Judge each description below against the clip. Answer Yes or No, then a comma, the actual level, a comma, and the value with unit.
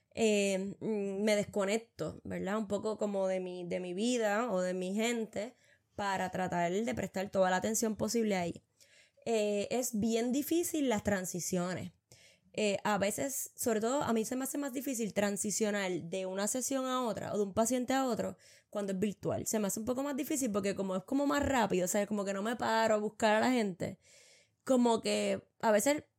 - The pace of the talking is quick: Yes, fast, 195 wpm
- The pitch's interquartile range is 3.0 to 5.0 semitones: Yes, average, 3.3 semitones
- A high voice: Yes, high, 210 Hz